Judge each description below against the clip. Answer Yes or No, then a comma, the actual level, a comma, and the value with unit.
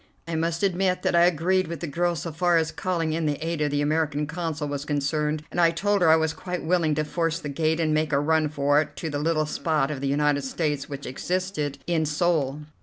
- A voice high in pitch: No, medium, 160 Hz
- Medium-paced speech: No, fast, 245 wpm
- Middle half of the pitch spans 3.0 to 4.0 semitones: No, narrow, 2.4 semitones